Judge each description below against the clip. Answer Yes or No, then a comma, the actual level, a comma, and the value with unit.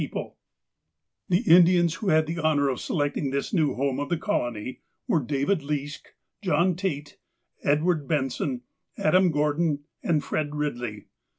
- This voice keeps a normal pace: Yes, average, 160 wpm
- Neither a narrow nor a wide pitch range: Yes, average, 3.3 semitones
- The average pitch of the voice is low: No, medium, 150 Hz